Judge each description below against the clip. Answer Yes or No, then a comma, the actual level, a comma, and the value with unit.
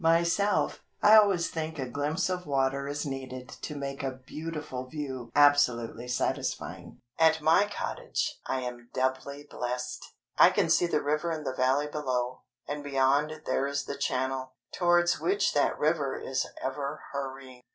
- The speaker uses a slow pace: No, average, 155 wpm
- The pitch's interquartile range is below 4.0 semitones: Yes, average, 3.2 semitones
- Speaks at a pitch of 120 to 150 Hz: Yes, medium, 140 Hz